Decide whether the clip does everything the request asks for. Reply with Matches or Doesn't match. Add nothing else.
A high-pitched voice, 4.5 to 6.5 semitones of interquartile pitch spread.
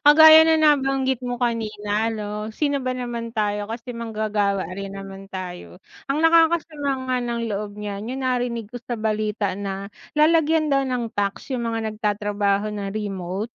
Doesn't match